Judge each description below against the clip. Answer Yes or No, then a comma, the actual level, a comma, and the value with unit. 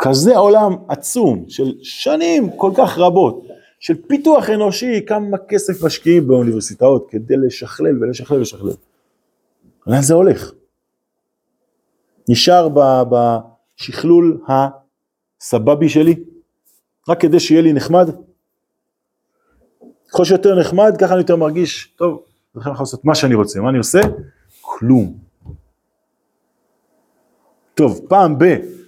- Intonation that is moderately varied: No, wide, 6.6 semitones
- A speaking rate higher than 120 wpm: No, average, 110 wpm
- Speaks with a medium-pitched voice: Yes, medium, 160 Hz